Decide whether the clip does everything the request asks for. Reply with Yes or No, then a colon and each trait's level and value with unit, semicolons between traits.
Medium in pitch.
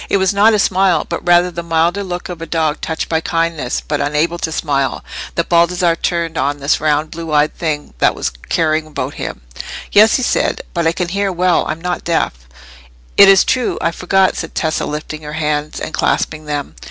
Yes: medium, 165 Hz